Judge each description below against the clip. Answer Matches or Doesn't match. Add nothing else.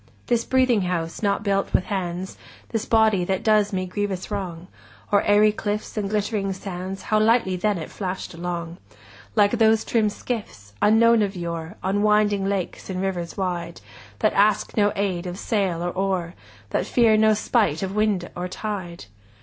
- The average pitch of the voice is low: Doesn't match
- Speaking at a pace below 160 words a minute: Doesn't match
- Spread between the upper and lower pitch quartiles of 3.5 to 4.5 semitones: Doesn't match